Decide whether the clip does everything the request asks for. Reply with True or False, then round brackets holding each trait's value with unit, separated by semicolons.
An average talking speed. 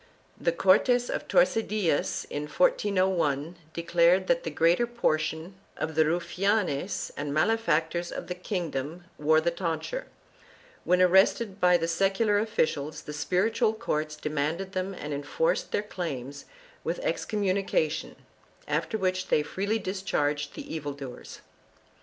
False (130 wpm)